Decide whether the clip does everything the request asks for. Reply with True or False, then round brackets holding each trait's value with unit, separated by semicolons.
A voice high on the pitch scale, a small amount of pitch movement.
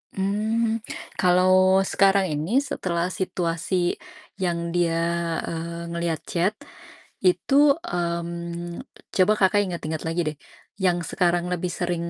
False (175 Hz; 1.8 semitones)